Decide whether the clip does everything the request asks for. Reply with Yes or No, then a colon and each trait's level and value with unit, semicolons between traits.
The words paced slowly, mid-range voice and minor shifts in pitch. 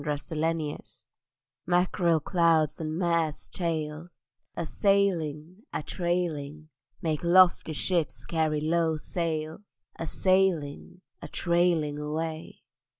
Yes: slow, 100 wpm; medium, 165 Hz; narrow, 2.1 semitones